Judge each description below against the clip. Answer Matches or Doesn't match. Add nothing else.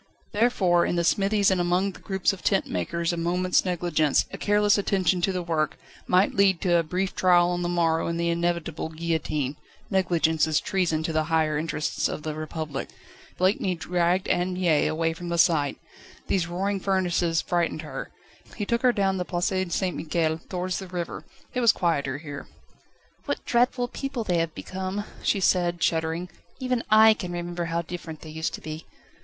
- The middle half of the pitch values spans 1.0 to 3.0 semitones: Matches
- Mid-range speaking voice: Matches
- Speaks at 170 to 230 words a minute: Matches